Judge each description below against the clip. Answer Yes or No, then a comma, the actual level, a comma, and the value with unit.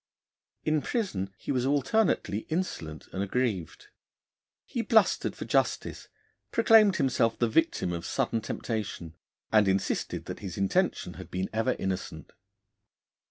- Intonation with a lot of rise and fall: Yes, wide, 8.4 semitones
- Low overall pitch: Yes, low, 115 Hz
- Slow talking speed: Yes, slow, 125 wpm